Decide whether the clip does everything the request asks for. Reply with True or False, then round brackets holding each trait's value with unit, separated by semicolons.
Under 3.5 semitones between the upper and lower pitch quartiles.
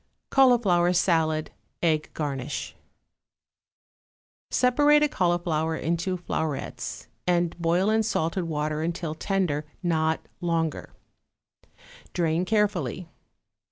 True (2.8 semitones)